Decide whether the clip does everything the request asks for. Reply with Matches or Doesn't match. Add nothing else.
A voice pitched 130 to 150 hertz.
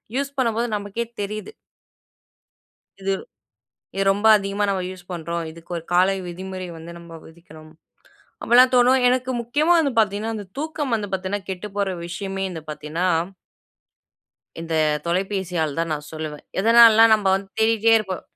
Doesn't match